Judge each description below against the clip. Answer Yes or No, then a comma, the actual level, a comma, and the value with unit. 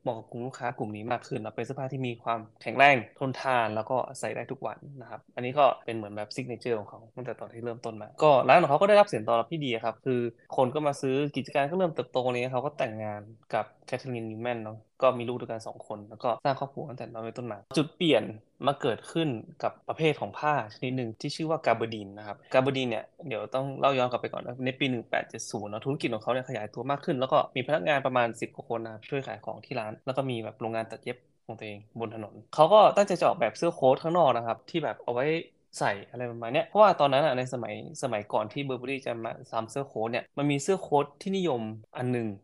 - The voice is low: Yes, low, 125 Hz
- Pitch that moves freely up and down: No, average, 3.7 semitones